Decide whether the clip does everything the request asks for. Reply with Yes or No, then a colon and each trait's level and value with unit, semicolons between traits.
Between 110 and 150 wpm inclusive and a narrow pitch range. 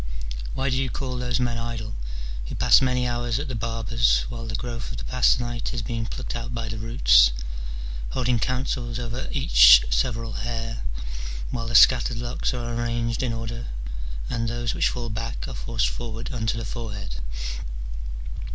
No: average, 175 wpm; narrow, 1.3 semitones